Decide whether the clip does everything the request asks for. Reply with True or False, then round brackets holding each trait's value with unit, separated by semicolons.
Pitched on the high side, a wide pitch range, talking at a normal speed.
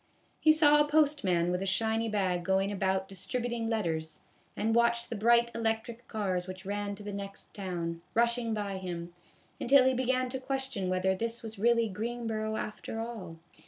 False (220 Hz; 3.7 semitones; 170 wpm)